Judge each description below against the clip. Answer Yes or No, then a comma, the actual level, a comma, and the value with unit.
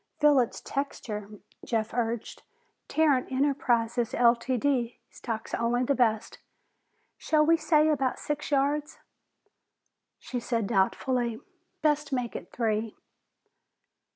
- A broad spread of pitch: No, average, 3.7 semitones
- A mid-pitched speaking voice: No, very high, 250 Hz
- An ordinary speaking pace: No, slow, 105 wpm